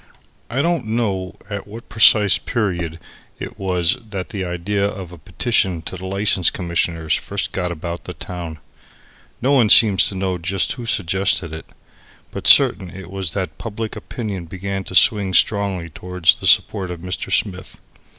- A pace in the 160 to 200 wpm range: Yes, average, 165 wpm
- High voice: No, very low, 95 Hz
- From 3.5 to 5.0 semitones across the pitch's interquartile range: No, average, 2.8 semitones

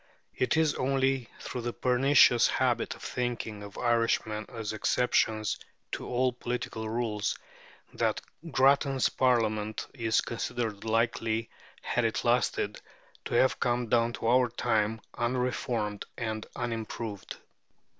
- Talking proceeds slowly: Yes, slow, 120 wpm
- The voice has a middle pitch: No, low, 120 Hz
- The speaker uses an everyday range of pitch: No, narrow, 2.2 semitones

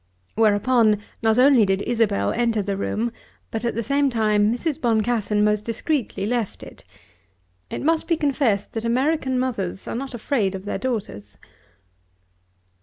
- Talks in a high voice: Yes, high, 225 Hz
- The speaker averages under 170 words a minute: Yes, average, 150 wpm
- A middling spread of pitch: Yes, average, 3.6 semitones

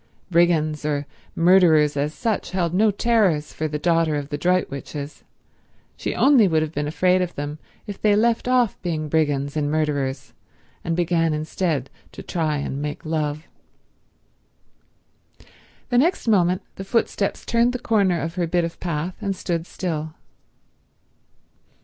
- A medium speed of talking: Yes, average, 150 wpm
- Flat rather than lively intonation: No, average, 4.0 semitones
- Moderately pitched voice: Yes, medium, 165 Hz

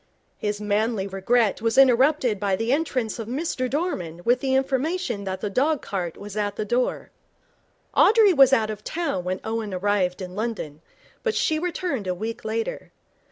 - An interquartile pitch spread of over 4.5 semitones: Yes, average, 5.0 semitones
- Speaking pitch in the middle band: No, high, 225 Hz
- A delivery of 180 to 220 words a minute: No, average, 170 wpm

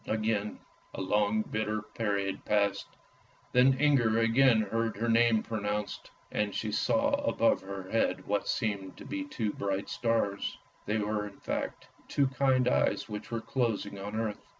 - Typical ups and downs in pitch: No, narrow, 2.3 semitones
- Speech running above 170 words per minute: No, average, 150 wpm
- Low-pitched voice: Yes, low, 110 Hz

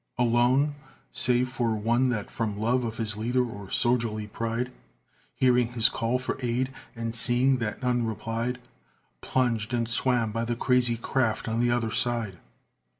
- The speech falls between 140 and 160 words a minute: Yes, average, 155 wpm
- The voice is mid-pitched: No, low, 120 Hz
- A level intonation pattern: Yes, narrow, 1.7 semitones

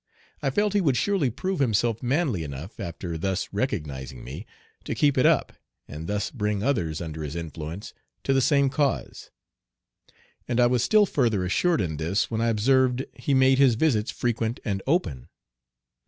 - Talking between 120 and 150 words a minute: No, average, 170 wpm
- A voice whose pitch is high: No, low, 115 Hz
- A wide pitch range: Yes, wide, 7.5 semitones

